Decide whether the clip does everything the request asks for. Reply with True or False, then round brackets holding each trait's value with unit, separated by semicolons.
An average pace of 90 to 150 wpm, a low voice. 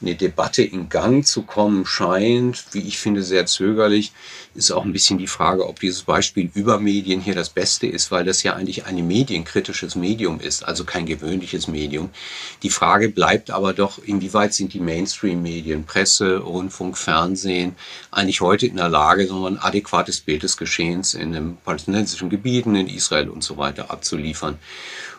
False (170 wpm; 95 Hz)